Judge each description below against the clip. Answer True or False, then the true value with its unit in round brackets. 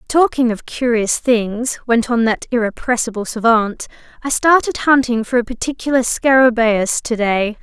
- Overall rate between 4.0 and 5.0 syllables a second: True (4.6 syllables/s)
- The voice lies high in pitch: True (240 Hz)